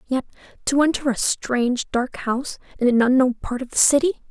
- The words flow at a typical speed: Yes, average, 180 wpm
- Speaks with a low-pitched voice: No, very high, 255 Hz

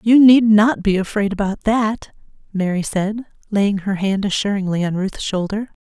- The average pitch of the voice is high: Yes, high, 205 Hz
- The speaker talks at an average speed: Yes, average, 165 wpm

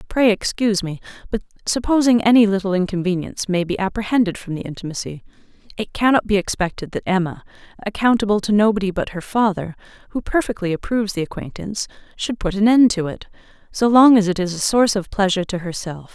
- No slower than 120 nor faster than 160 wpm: No, average, 180 wpm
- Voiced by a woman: Yes, female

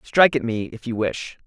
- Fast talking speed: Yes, fast, 245 wpm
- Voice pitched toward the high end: No, low, 125 Hz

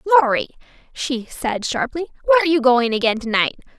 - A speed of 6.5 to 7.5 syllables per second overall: Yes, 6.8 syllables/s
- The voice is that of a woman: Yes, female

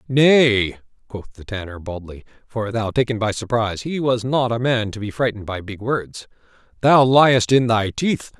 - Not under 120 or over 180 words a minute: Yes, average, 170 wpm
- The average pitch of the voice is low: Yes, low, 115 Hz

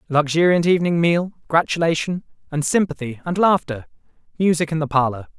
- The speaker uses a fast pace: No, slow, 135 wpm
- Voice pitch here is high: No, medium, 160 Hz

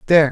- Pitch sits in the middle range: Yes, medium, 155 Hz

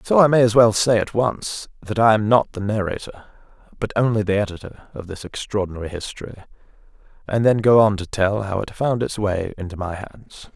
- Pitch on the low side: Yes, low, 105 Hz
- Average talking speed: No, fast, 210 wpm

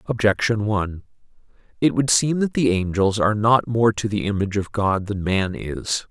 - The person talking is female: No, male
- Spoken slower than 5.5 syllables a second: Yes, 5.0 syllables/s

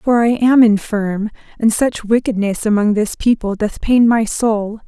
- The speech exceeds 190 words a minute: No, average, 170 wpm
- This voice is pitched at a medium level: No, high, 220 Hz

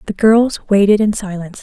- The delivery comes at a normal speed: Yes, average, 185 wpm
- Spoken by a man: No, female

